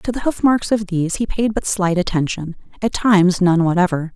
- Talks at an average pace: No, fast, 215 wpm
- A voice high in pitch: Yes, high, 195 Hz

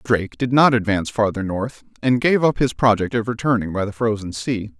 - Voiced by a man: Yes, male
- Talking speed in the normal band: No, fast, 215 wpm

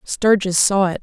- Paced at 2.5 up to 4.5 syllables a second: Yes, 4.3 syllables/s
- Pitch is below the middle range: No, high, 195 Hz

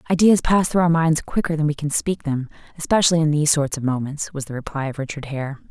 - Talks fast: Yes, fast, 240 wpm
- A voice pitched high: No, medium, 150 Hz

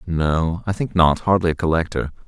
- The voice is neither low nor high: No, very low, 85 Hz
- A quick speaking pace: No, average, 185 wpm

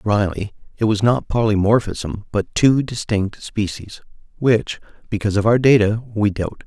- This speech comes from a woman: No, male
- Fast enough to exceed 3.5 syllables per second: Yes, 4.6 syllables/s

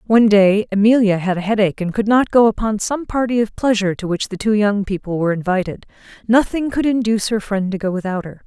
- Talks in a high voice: Yes, high, 210 Hz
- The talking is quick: Yes, fast, 225 wpm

